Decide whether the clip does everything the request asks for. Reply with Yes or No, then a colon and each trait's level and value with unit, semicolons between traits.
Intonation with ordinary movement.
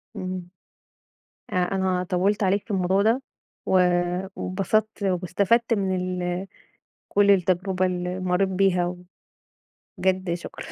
No: narrow, 1.6 semitones